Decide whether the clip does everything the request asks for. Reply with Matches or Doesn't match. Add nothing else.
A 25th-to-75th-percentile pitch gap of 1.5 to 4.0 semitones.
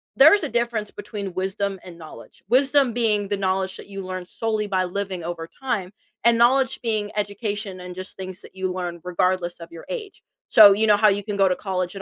Matches